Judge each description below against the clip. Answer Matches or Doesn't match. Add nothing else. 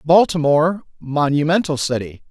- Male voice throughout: Matches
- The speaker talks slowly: Matches